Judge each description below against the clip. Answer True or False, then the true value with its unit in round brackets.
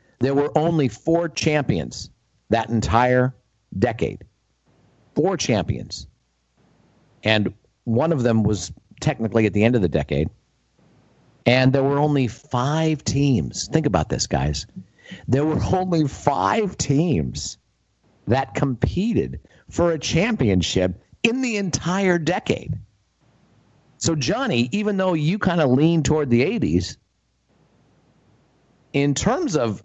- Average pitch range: False (6.2 semitones)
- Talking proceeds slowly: True (120 wpm)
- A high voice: False (135 Hz)